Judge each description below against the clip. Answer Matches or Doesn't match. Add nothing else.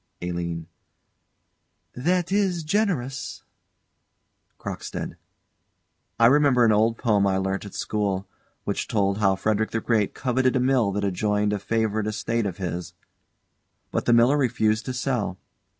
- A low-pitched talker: Matches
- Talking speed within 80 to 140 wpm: Matches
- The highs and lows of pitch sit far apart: Doesn't match